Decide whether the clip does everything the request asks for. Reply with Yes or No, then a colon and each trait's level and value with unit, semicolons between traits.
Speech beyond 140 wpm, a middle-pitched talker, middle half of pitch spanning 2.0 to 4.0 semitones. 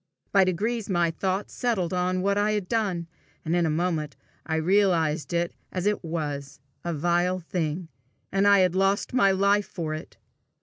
Yes: average, 175 wpm; medium, 180 Hz; average, 3.1 semitones